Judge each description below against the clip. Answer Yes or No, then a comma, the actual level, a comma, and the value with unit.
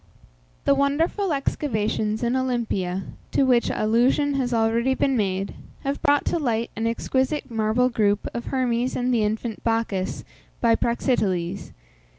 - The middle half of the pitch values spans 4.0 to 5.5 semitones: No, average, 3.4 semitones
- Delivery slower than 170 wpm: Yes, average, 140 wpm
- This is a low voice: No, high, 235 Hz